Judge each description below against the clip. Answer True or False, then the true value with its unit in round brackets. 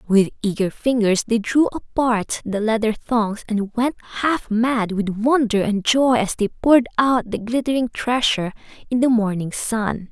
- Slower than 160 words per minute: False (165 wpm)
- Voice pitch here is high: True (225 Hz)